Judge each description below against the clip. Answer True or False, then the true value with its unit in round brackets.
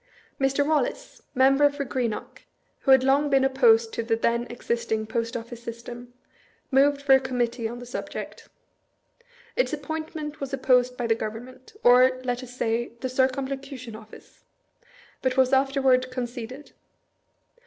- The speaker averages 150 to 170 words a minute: True (155 wpm)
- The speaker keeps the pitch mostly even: True (2.3 semitones)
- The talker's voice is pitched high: True (255 Hz)